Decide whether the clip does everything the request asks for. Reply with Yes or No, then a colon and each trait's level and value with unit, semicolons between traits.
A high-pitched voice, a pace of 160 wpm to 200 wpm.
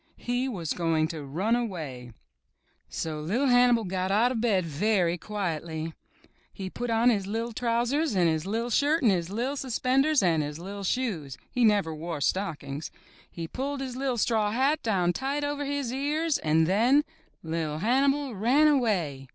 Yes: high, 215 Hz; average, 175 wpm